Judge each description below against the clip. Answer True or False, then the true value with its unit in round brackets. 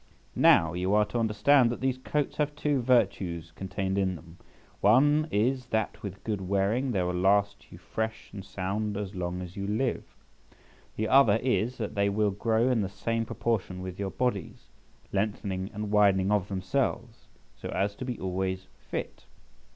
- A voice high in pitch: False (105 Hz)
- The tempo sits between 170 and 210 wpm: True (175 wpm)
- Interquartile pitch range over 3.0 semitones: True (3.6 semitones)